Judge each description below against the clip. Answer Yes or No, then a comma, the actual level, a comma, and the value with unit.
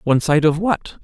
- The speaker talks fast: Yes, fast, 230 wpm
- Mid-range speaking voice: Yes, medium, 165 Hz